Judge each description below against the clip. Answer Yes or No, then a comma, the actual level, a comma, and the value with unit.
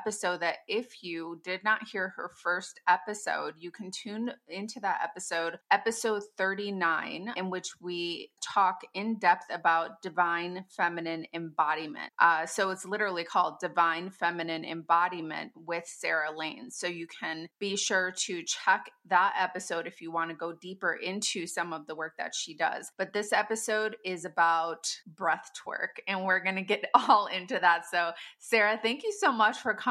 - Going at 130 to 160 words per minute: No, average, 170 wpm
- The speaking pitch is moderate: Yes, medium, 180 Hz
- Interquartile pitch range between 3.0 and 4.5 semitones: Yes, average, 3.6 semitones